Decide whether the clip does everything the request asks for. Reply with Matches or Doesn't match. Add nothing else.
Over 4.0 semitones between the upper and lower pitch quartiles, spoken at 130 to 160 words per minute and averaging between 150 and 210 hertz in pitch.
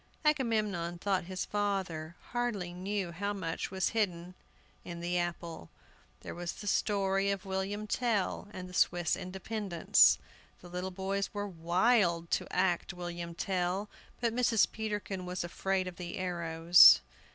Doesn't match